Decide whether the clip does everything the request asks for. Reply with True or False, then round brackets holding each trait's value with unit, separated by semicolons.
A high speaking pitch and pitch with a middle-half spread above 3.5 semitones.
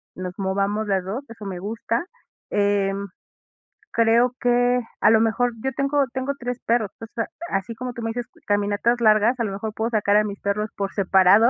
False (220 Hz; 3.1 semitones)